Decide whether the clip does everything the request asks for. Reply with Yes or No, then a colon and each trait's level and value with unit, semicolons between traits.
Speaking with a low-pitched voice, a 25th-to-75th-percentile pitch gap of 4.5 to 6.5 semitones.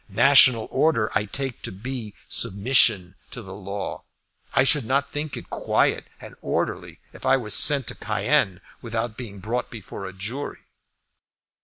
Yes: low, 115 Hz; average, 4.9 semitones